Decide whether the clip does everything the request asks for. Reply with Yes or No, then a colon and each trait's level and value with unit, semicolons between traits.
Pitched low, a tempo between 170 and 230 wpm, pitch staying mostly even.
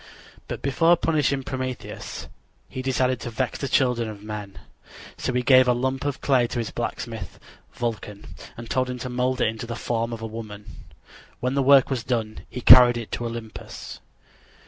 Yes: low, 125 Hz; average, 185 wpm; narrow, 2.3 semitones